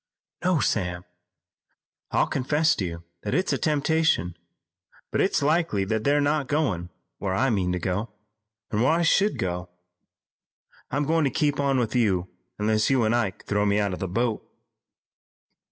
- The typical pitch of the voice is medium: No, low, 115 Hz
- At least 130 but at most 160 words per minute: No, average, 170 wpm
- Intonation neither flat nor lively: No, wide, 7.4 semitones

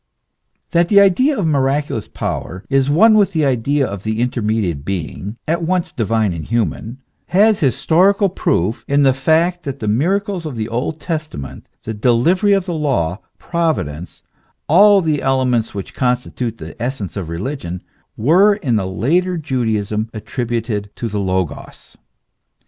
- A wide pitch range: Yes, wide, 7.7 semitones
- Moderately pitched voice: No, low, 130 Hz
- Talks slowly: No, average, 150 wpm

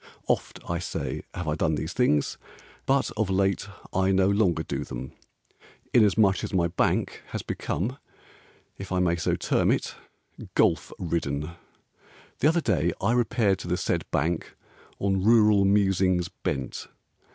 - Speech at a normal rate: Yes, average, 150 wpm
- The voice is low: Yes, very low, 95 Hz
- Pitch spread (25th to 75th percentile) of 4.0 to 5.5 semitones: No, average, 3.4 semitones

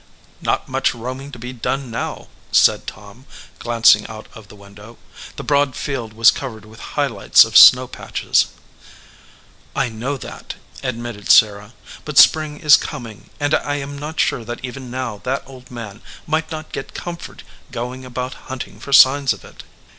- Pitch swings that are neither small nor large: Yes, average, 3.6 semitones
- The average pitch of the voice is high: No, low, 125 Hz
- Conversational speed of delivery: Yes, average, 170 wpm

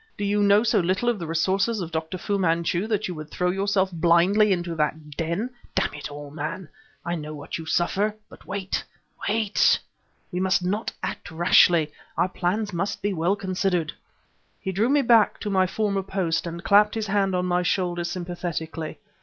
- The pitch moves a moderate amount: Yes, average, 3.1 semitones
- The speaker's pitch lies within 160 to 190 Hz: Yes, medium, 185 Hz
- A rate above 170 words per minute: Yes, average, 185 wpm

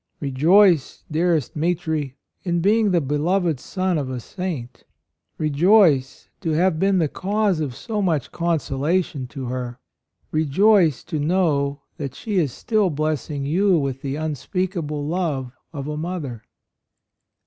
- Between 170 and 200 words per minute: No, slow, 135 wpm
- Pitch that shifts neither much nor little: Yes, average, 4.6 semitones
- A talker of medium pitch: Yes, medium, 155 Hz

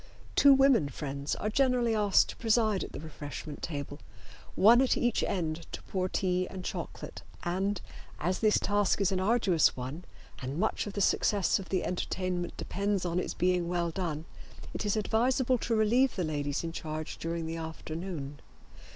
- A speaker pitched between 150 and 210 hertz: Yes, medium, 185 Hz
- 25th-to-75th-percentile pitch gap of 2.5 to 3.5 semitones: No, average, 4.8 semitones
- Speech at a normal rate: Yes, average, 175 wpm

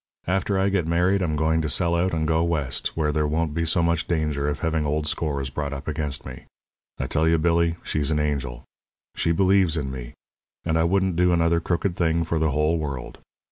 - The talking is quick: Yes, fast, 215 wpm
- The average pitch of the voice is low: Yes, very low, 80 Hz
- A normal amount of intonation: No, narrow, 2.1 semitones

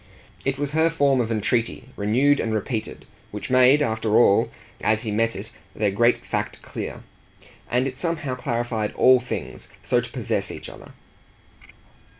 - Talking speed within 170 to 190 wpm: No, average, 155 wpm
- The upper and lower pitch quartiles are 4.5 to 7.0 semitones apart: No, average, 3.5 semitones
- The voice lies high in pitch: No, low, 120 Hz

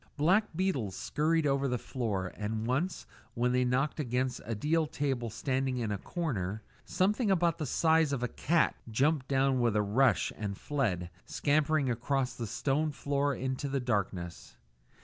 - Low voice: Yes, low, 130 Hz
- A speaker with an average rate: Yes, average, 165 wpm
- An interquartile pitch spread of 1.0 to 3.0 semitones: No, average, 4.5 semitones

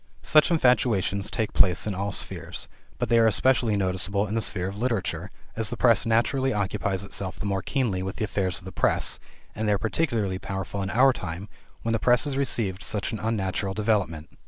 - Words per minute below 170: No, fast, 205 wpm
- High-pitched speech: No, low, 105 Hz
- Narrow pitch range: No, average, 3.3 semitones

